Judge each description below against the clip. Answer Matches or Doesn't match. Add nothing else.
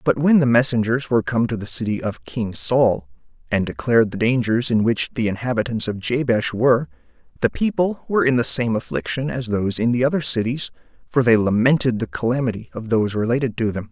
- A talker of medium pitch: Doesn't match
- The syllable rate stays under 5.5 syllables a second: Doesn't match